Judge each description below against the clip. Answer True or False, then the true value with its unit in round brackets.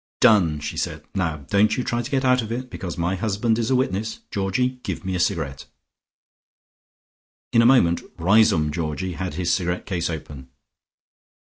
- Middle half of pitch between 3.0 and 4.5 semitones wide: False (5.4 semitones)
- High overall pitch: False (95 Hz)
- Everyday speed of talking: True (175 wpm)